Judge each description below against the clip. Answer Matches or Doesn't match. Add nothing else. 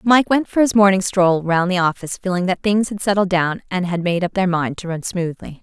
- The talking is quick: Matches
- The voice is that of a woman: Matches